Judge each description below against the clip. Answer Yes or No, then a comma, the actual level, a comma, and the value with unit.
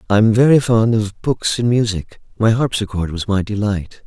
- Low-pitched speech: Yes, low, 110 Hz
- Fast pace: No, average, 190 wpm